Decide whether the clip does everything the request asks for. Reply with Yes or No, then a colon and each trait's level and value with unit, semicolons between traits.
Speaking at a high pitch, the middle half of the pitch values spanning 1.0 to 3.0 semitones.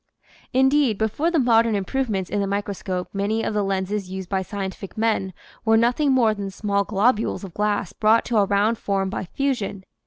Yes: high, 210 Hz; average, 2.7 semitones